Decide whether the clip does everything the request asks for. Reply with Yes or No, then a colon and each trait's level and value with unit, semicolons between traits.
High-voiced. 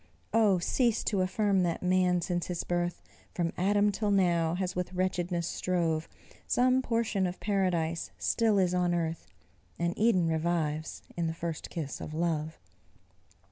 No: medium, 180 Hz